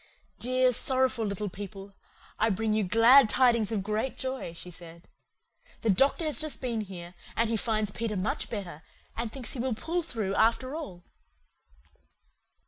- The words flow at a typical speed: Yes, average, 160 wpm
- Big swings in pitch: No, average, 4.5 semitones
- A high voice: Yes, high, 225 Hz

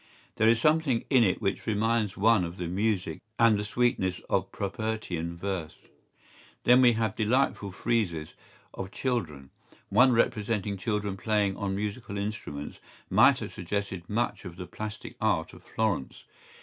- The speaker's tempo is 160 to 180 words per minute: No, average, 150 wpm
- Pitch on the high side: No, low, 105 Hz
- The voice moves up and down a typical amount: Yes, average, 3.4 semitones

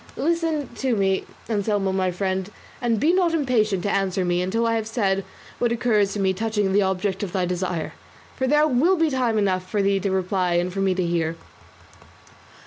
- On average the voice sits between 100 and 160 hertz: No, high, 200 Hz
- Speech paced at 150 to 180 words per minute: No, fast, 205 wpm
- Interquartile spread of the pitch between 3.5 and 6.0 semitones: Yes, average, 3.9 semitones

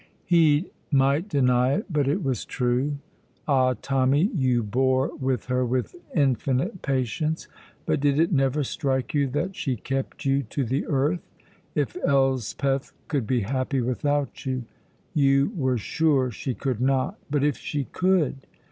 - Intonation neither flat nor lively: No, narrow, 2.2 semitones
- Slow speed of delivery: No, average, 150 wpm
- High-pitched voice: No, low, 135 Hz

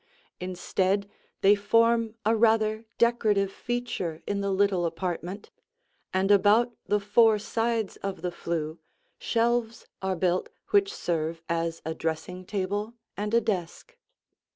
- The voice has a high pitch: Yes, high, 200 Hz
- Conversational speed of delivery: No, slow, 130 wpm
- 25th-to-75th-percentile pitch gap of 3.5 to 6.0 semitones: Yes, average, 3.9 semitones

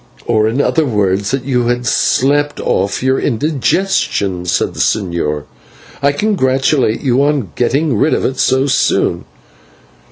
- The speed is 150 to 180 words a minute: No, average, 140 wpm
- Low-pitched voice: Yes, low, 130 Hz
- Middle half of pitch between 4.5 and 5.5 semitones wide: Yes, average, 4.9 semitones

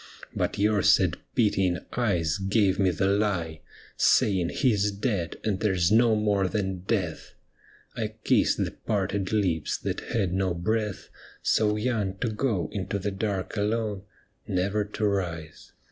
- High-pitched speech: No, low, 100 Hz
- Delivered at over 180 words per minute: No, average, 150 wpm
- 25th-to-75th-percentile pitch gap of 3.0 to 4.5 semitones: No, narrow, 2.4 semitones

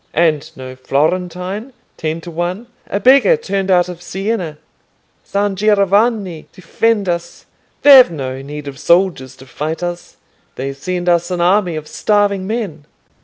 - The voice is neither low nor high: Yes, medium, 180 Hz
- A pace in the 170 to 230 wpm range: No, average, 145 wpm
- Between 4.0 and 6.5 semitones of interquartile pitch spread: Yes, average, 4.3 semitones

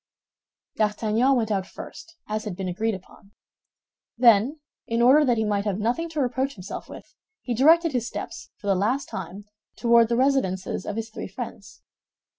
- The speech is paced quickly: No, average, 175 wpm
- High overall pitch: Yes, high, 225 Hz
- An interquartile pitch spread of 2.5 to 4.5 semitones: Yes, average, 4.2 semitones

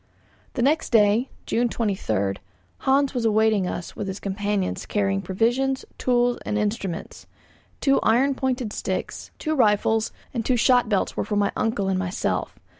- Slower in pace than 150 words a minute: No, average, 155 wpm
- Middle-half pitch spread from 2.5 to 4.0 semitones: Yes, average, 3.6 semitones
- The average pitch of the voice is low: No, high, 220 Hz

